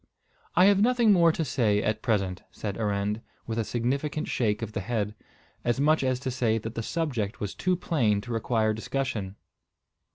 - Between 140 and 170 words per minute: No, average, 185 wpm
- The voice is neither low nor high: No, low, 115 Hz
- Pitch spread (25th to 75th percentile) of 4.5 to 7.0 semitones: Yes, average, 4.9 semitones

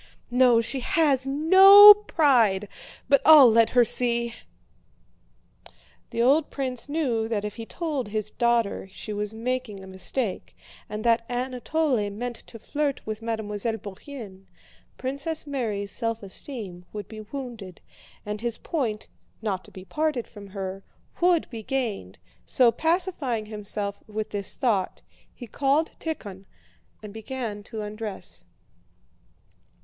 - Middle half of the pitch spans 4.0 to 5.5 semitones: Yes, average, 4.4 semitones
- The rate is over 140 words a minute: No, slow, 135 wpm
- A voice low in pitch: No, high, 230 Hz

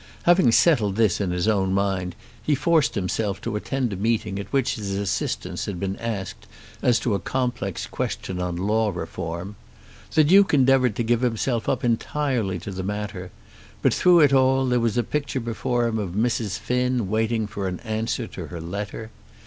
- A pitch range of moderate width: Yes, average, 4.3 semitones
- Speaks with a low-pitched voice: Yes, low, 110 Hz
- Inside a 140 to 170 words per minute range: No, average, 185 wpm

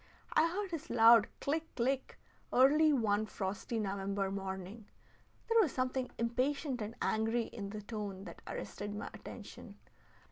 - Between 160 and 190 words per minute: No, average, 140 wpm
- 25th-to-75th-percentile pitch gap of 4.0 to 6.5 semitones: Yes, average, 4.8 semitones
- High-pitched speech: Yes, high, 230 Hz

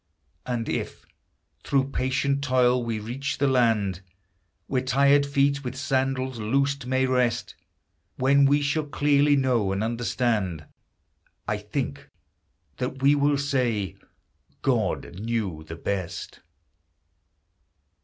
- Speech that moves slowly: Yes, slow, 115 wpm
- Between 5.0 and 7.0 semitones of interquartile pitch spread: No, average, 3.3 semitones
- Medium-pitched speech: No, low, 130 Hz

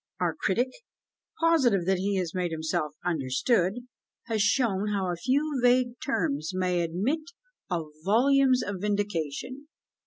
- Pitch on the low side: No, high, 200 Hz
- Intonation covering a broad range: Yes, wide, 6.3 semitones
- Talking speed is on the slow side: Yes, slow, 130 wpm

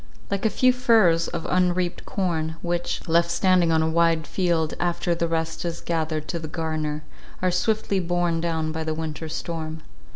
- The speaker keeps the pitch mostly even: Yes, narrow, 1.7 semitones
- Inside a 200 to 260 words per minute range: No, average, 175 wpm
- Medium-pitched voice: Yes, medium, 170 Hz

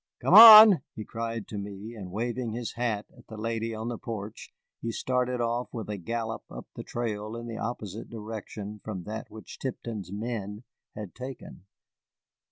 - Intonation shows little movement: Yes, narrow, 2.1 semitones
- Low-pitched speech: Yes, low, 115 Hz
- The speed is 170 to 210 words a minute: Yes, average, 175 wpm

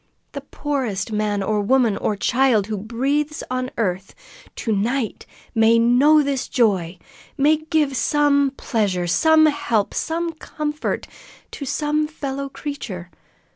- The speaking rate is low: Yes, slow, 130 wpm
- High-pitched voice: Yes, very high, 255 Hz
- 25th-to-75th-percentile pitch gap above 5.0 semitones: Yes, wide, 5.6 semitones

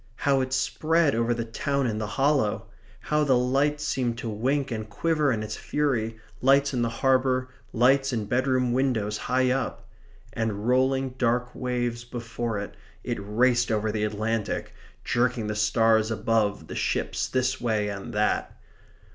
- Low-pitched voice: Yes, low, 120 Hz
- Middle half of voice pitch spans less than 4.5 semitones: Yes, average, 3.2 semitones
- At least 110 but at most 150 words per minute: No, average, 160 wpm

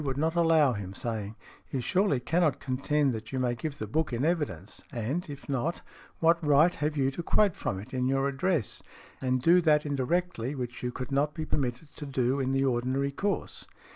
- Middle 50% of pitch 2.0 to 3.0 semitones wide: No, average, 3.9 semitones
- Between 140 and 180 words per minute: No, fast, 205 wpm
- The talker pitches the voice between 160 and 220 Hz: No, medium, 140 Hz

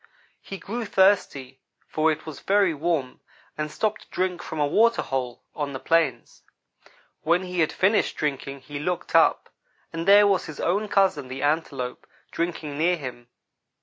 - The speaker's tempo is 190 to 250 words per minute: No, average, 165 wpm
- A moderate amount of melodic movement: Yes, average, 5.0 semitones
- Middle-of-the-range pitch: Yes, medium, 160 Hz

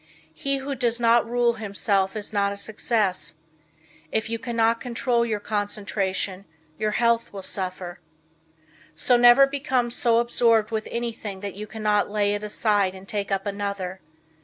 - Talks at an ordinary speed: Yes, average, 155 wpm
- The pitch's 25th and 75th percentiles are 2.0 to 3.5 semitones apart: Yes, average, 2.8 semitones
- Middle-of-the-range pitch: No, high, 215 Hz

